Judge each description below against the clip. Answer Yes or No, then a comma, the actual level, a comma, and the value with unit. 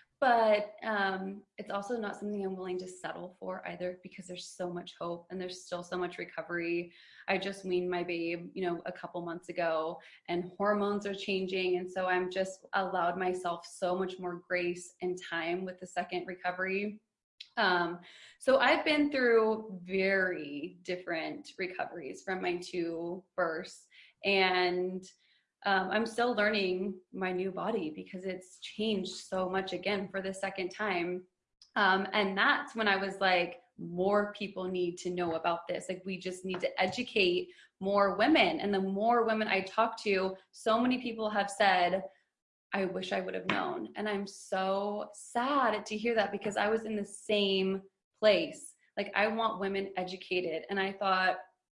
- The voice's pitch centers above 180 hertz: Yes, high, 190 Hz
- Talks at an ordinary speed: Yes, average, 170 wpm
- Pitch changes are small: Yes, narrow, 2.3 semitones